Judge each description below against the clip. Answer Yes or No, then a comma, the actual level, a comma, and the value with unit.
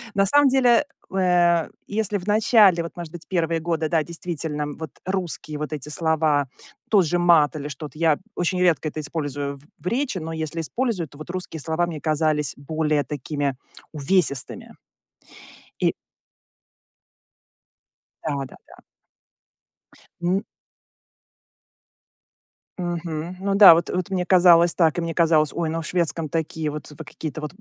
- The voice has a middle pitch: Yes, medium, 165 Hz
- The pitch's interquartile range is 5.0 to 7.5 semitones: No, average, 2.8 semitones